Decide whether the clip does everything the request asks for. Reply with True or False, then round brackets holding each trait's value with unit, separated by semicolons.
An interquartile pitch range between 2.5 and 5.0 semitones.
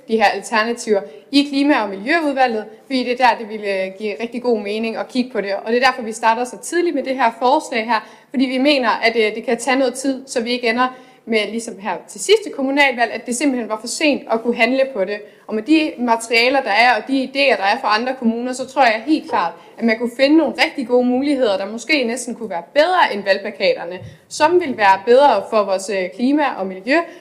True (3.6 semitones)